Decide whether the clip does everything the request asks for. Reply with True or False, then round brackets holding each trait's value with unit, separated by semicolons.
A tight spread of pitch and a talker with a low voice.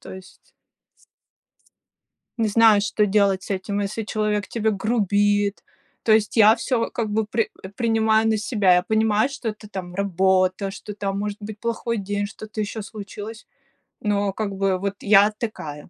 False (1.7 semitones; 210 Hz)